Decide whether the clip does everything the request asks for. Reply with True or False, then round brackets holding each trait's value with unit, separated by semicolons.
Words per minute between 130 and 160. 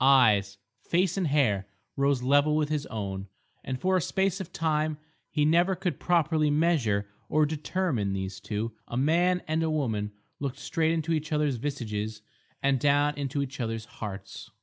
False (170 wpm)